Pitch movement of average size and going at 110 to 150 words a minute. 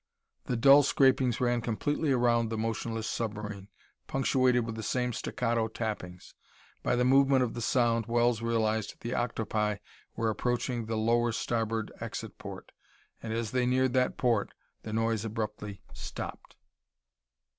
No: narrow, 1.9 semitones; average, 145 wpm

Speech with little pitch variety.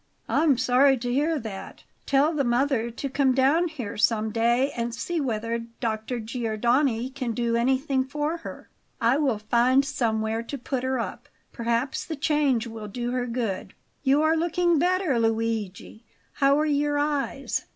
No: average, 3.7 semitones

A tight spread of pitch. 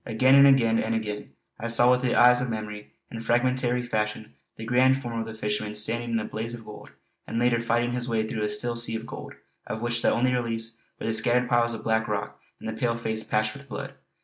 Yes: narrow, 1.7 semitones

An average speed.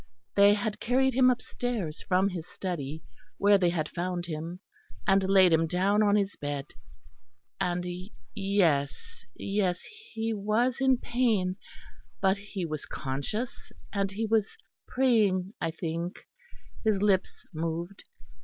No: slow, 130 wpm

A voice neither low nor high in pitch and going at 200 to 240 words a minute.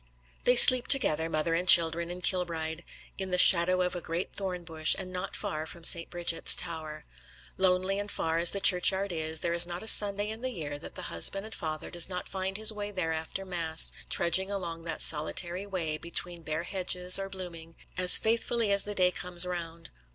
Yes: medium, 180 Hz; fast, 205 wpm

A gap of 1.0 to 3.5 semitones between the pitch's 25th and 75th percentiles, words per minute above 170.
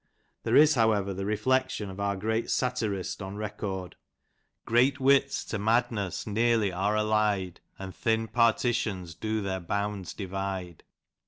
No: average, 3.0 semitones; average, 140 wpm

